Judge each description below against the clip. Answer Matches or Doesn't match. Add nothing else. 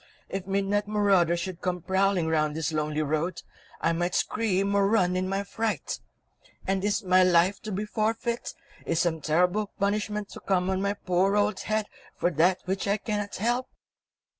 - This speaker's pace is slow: Doesn't match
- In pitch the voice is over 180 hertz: Matches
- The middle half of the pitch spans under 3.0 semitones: Matches